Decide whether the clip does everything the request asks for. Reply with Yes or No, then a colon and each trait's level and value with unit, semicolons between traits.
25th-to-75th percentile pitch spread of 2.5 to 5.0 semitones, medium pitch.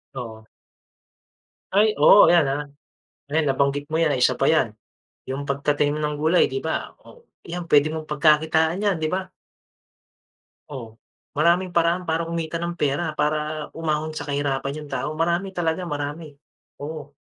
Yes: average, 2.8 semitones; medium, 155 Hz